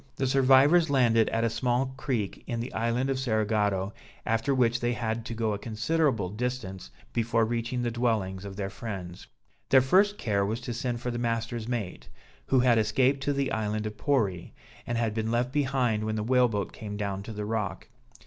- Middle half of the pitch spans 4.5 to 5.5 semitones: No, average, 3.0 semitones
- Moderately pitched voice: No, low, 115 Hz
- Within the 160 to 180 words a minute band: No, average, 200 wpm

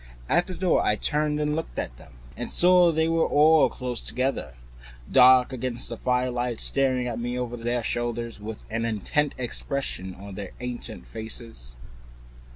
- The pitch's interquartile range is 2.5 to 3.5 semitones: No, average, 4.2 semitones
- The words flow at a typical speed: Yes, average, 165 wpm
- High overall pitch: No, low, 125 Hz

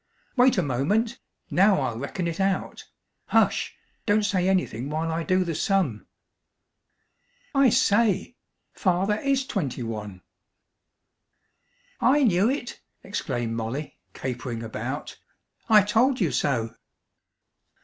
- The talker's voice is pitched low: No, medium, 185 Hz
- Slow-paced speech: Yes, slow, 115 wpm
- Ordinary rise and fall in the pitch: No, wide, 8.5 semitones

